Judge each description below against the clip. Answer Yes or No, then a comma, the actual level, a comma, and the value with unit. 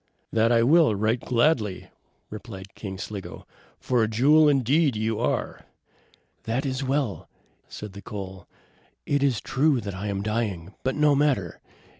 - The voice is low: Yes, low, 115 Hz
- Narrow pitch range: No, average, 5.2 semitones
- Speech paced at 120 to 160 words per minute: Yes, average, 150 wpm